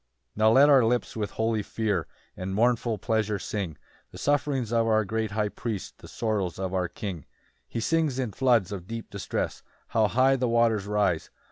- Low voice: Yes, low, 110 Hz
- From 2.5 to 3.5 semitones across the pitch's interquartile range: Yes, average, 2.8 semitones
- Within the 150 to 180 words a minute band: No, average, 195 wpm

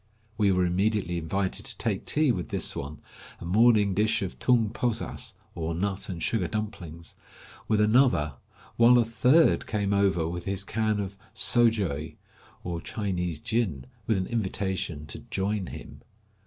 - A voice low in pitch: Yes, low, 100 Hz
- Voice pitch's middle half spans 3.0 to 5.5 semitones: Yes, average, 4.0 semitones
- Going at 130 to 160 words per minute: Yes, average, 155 wpm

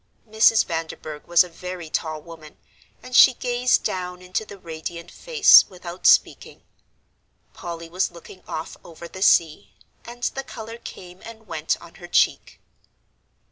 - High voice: No, medium, 180 Hz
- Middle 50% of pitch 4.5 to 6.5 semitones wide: Yes, average, 4.8 semitones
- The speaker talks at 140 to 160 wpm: Yes, average, 145 wpm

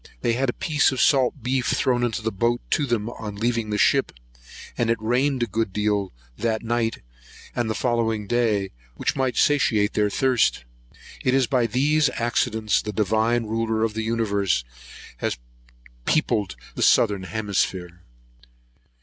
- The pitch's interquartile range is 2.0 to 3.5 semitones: Yes, narrow, 2.5 semitones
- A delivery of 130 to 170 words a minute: Yes, average, 160 wpm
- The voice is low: Yes, low, 115 Hz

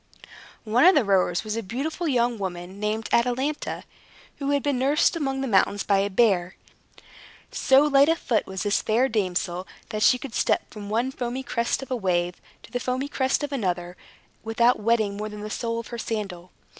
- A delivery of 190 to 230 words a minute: Yes, average, 195 wpm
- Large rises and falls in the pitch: No, average, 4.7 semitones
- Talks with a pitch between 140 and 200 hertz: No, high, 230 Hz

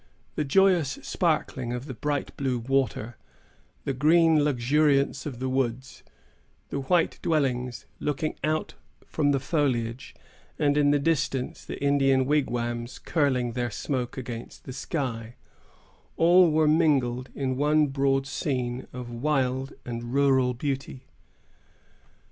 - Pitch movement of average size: Yes, average, 3.0 semitones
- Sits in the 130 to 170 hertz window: Yes, low, 135 Hz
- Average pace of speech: No, slow, 125 wpm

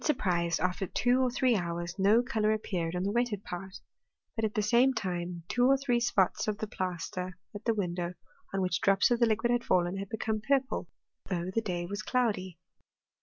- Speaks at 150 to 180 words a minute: No, average, 200 wpm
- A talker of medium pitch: No, high, 205 Hz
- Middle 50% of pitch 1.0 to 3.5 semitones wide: No, average, 4.8 semitones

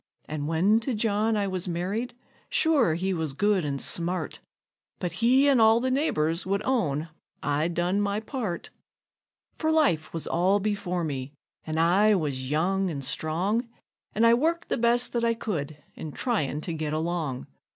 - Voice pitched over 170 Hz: Yes, medium, 185 Hz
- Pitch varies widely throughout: Yes, wide, 6.2 semitones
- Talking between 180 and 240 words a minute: No, average, 170 wpm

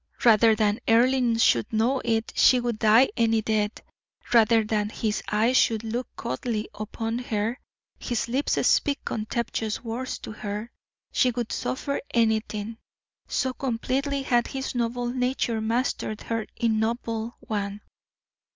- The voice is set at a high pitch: Yes, high, 230 Hz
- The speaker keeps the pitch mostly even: Yes, narrow, 2.1 semitones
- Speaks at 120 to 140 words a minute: Yes, slow, 135 wpm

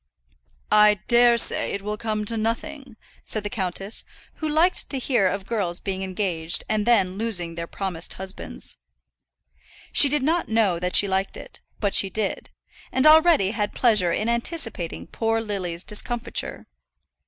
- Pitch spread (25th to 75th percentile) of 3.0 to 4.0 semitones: Yes, average, 3.7 semitones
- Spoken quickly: No, average, 155 wpm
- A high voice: Yes, high, 210 Hz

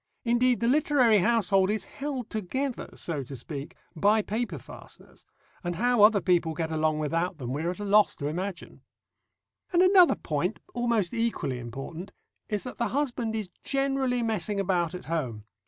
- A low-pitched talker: No, high, 205 Hz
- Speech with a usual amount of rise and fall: No, wide, 6.4 semitones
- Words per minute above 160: Yes, average, 170 wpm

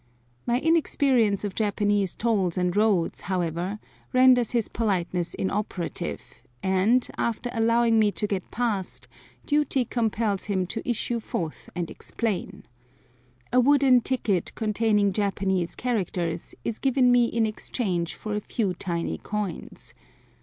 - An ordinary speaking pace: No, slow, 125 wpm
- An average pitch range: Yes, average, 4.0 semitones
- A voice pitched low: No, high, 210 Hz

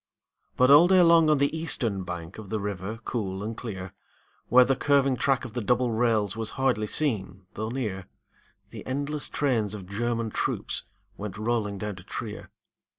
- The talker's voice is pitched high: No, low, 115 Hz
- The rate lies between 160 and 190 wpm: Yes, average, 175 wpm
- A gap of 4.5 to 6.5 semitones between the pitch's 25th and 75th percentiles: Yes, average, 4.8 semitones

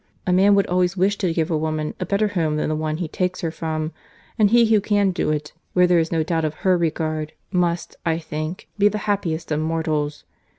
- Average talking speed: No, fast, 230 wpm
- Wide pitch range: No, average, 3.3 semitones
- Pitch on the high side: No, medium, 170 Hz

